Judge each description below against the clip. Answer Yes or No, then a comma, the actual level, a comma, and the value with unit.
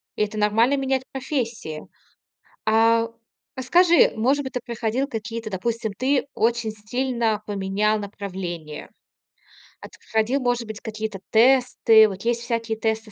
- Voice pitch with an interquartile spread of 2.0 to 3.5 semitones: Yes, narrow, 2.6 semitones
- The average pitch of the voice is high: Yes, high, 225 Hz